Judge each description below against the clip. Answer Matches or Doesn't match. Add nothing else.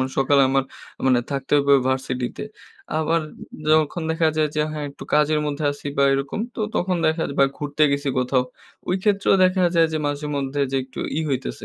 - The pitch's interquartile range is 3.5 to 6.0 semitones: Doesn't match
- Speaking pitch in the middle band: Matches